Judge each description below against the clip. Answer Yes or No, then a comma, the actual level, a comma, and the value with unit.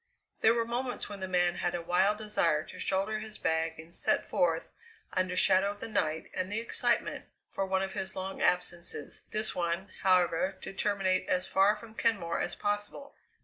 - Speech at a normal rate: Yes, average, 190 wpm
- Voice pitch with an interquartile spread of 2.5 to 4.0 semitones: Yes, average, 2.8 semitones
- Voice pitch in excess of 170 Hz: Yes, high, 190 Hz